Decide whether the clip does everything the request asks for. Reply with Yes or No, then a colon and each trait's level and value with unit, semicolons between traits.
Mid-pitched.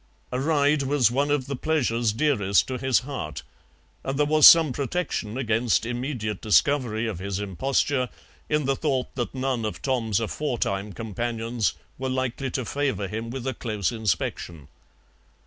No: low, 125 Hz